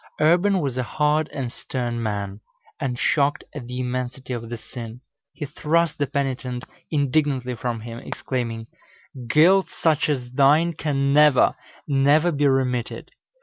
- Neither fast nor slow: Yes, average, 145 wpm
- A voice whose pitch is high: No, low, 135 Hz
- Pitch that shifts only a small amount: No, average, 3.4 semitones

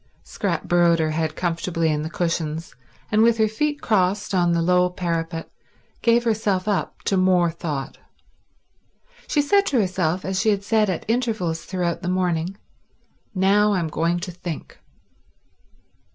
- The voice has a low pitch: No, medium, 180 Hz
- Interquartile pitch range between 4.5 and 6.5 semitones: No, average, 3.9 semitones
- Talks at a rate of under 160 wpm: Yes, average, 150 wpm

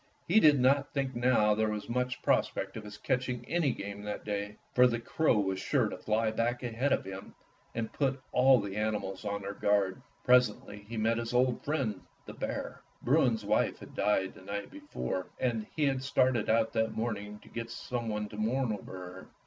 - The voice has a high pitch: No, low, 115 Hz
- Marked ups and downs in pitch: No, average, 3.5 semitones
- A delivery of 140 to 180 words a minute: No, average, 200 wpm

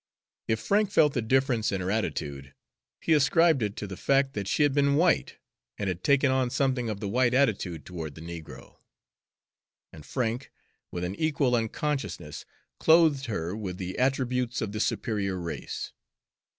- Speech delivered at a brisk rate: No, average, 165 wpm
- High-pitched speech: No, low, 115 Hz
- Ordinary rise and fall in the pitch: No, wide, 6.5 semitones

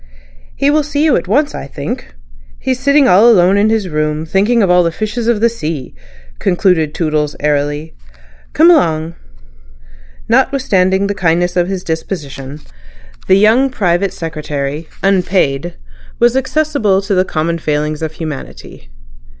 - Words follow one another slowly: No, average, 145 wpm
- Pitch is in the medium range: Yes, medium, 180 Hz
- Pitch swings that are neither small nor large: No, wide, 6.2 semitones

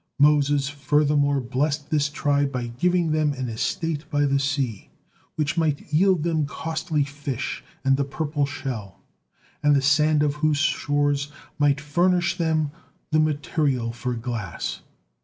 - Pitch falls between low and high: Yes, medium, 145 Hz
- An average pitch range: No, narrow, 2.0 semitones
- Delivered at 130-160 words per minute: Yes, average, 140 wpm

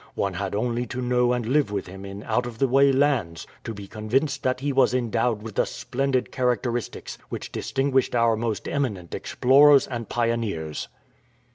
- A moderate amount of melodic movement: Yes, average, 3.4 semitones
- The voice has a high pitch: No, low, 120 Hz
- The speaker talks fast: No, average, 175 wpm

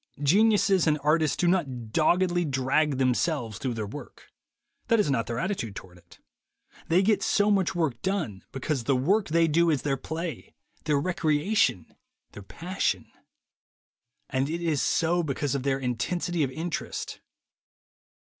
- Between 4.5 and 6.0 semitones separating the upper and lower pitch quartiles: Yes, average, 5.1 semitones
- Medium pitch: Yes, medium, 155 Hz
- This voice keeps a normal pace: Yes, average, 150 wpm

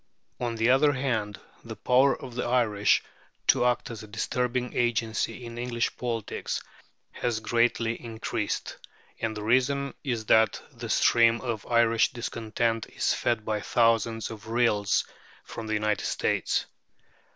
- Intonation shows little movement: Yes, narrow, 1.8 semitones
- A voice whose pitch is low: Yes, low, 115 Hz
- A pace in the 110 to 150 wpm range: Yes, average, 140 wpm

